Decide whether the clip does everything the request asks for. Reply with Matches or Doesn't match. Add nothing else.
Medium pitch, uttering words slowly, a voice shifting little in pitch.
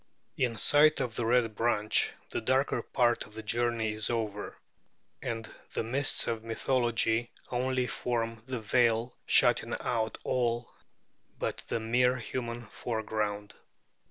Doesn't match